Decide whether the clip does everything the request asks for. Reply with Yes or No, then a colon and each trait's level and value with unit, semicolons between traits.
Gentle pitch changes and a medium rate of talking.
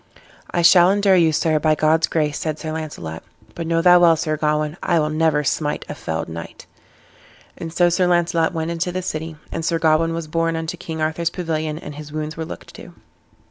No: narrow, 1.6 semitones; fast, 210 wpm